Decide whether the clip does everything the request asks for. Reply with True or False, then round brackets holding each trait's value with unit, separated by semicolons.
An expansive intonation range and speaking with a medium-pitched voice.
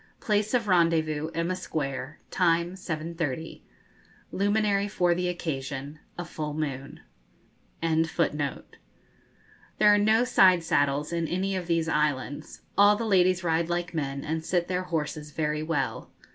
False (3.3 semitones; 165 Hz)